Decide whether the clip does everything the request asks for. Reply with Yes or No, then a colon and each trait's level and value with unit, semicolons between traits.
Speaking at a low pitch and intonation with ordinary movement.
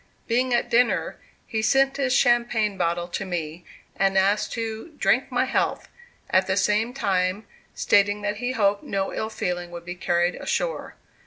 No: high, 205 Hz; average, 4.3 semitones